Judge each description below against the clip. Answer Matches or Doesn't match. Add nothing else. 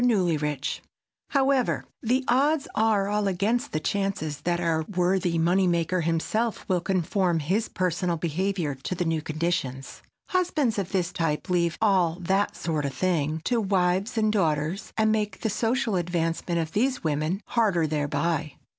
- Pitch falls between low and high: Matches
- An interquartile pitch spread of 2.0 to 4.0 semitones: Doesn't match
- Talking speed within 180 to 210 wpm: Doesn't match